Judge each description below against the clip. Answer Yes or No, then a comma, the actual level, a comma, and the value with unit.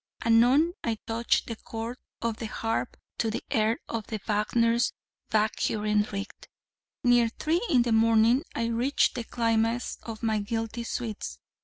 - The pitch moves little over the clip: Yes, narrow, 1.4 semitones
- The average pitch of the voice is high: Yes, high, 230 Hz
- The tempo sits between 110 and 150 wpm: Yes, average, 145 wpm